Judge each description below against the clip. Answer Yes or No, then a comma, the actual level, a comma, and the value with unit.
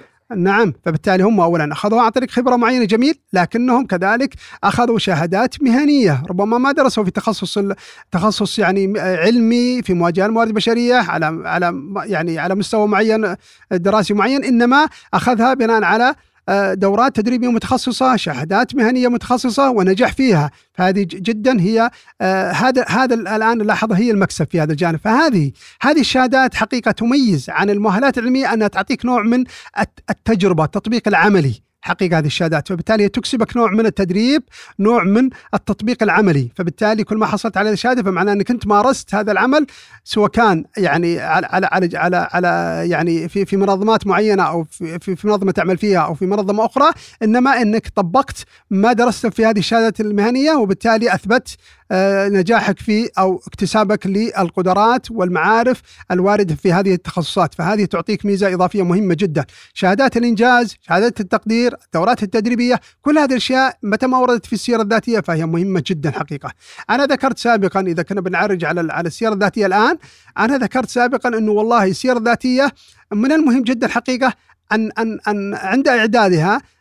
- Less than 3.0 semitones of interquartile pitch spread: No, average, 4.1 semitones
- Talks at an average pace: No, fast, 150 wpm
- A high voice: Yes, high, 215 Hz